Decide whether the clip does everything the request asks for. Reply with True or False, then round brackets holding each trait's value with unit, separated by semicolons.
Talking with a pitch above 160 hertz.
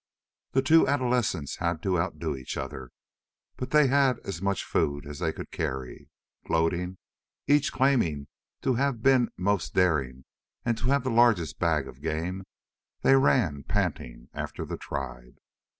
False (90 Hz)